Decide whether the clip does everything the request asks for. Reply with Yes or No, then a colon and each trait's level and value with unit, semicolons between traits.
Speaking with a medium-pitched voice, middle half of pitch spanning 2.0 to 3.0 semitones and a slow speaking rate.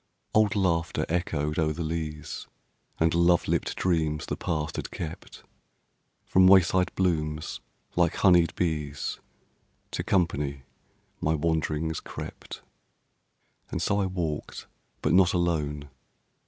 No: very low, 80 Hz; narrow, 2.6 semitones; slow, 115 wpm